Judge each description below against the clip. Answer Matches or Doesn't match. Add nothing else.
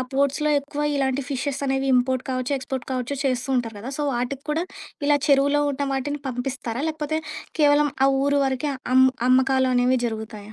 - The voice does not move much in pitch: Matches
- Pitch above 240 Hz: Matches